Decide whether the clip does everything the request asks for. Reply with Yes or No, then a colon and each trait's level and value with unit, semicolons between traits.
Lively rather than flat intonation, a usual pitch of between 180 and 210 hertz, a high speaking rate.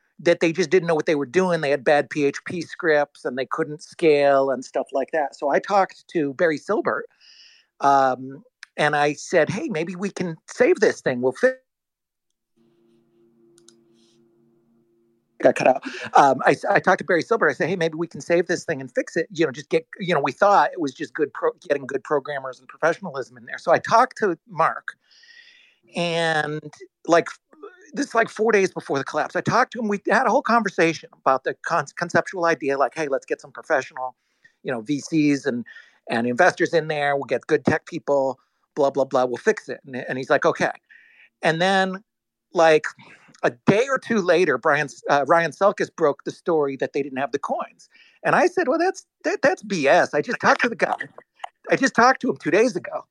No: wide, 6.5 semitones; medium, 165 Hz; fast, 210 wpm